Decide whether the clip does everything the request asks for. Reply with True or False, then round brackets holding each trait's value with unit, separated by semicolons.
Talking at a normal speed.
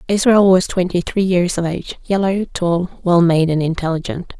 True (180 wpm)